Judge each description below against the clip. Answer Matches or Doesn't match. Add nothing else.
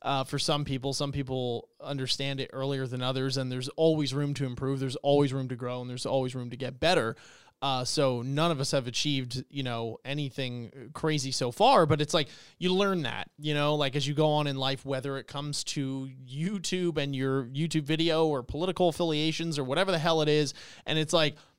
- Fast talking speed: Matches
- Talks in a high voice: Doesn't match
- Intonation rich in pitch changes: Doesn't match